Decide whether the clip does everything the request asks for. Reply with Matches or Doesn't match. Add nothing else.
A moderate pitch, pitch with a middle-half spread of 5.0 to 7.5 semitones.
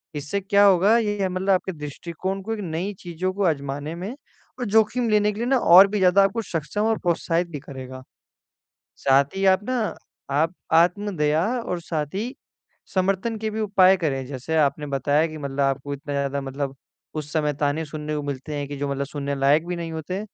Matches